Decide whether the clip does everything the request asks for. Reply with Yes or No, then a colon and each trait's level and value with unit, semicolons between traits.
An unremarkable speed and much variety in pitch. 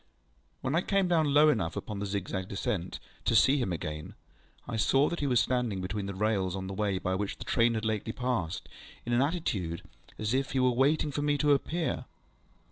No: fast, 210 wpm; wide, 6.5 semitones